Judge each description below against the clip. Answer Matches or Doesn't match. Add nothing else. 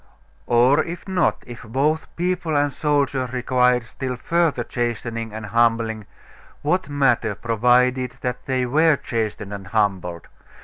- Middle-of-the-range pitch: Doesn't match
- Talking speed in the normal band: Doesn't match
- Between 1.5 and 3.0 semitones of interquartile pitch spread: Doesn't match